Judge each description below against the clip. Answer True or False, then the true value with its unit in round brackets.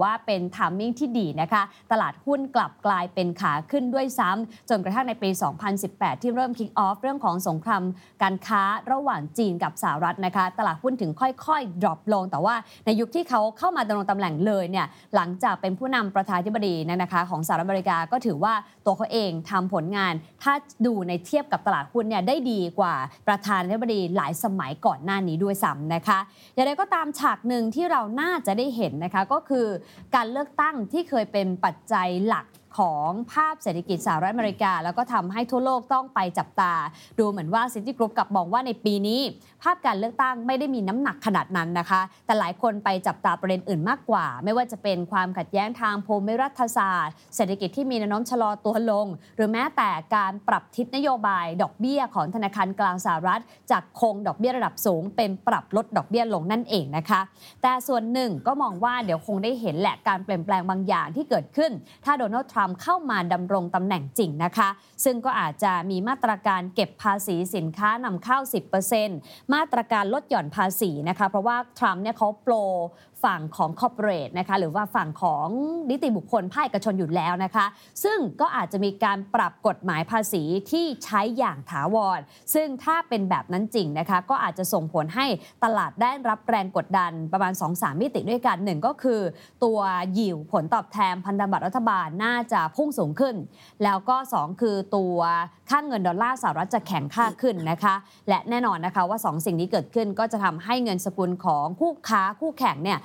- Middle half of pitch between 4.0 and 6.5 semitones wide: True (4.6 semitones)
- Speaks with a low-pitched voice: False (210 Hz)